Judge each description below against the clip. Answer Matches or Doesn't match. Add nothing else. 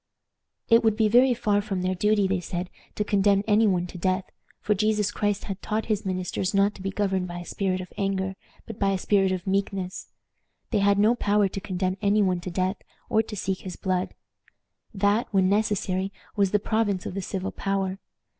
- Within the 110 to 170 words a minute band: Doesn't match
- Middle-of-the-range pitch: Doesn't match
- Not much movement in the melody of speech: Matches